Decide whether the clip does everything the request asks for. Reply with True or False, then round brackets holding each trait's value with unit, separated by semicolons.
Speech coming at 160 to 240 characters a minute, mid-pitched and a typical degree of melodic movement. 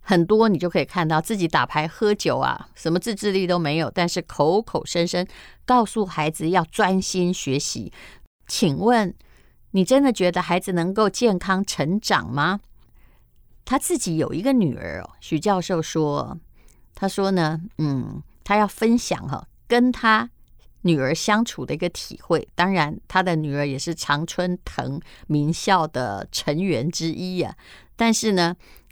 True (230 characters per minute; 180 Hz; 4.7 semitones)